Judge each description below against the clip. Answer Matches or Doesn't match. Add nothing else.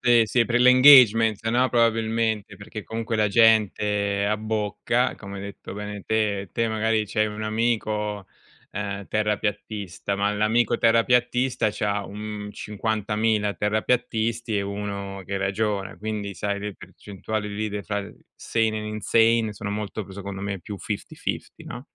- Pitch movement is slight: Matches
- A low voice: Matches